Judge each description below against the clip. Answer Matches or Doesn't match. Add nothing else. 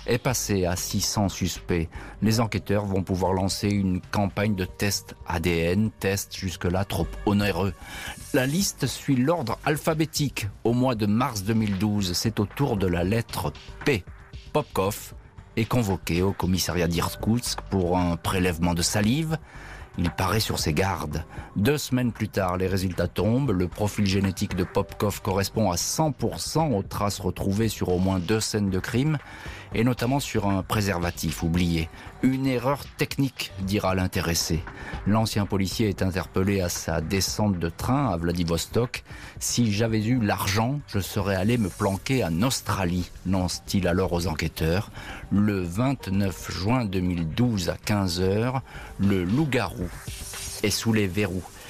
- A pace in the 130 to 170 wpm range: Matches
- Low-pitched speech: Matches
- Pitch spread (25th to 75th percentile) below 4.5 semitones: Matches